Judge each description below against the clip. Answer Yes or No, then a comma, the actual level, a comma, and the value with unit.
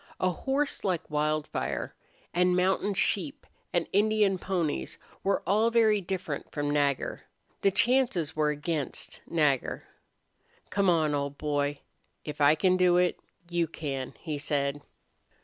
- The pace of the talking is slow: Yes, slow, 130 wpm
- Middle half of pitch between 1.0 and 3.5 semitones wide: No, average, 4.6 semitones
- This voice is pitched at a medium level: Yes, medium, 170 Hz